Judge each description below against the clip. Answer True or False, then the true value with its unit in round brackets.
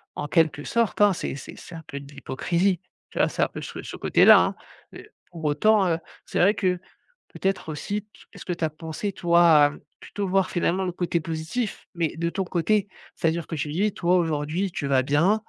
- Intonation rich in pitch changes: False (3.6 semitones)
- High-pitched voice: False (170 Hz)